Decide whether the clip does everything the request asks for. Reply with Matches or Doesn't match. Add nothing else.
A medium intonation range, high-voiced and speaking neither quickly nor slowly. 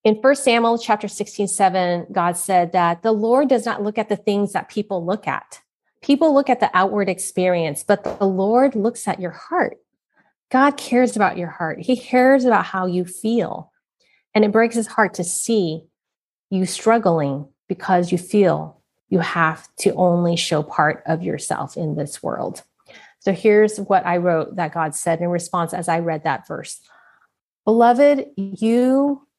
Matches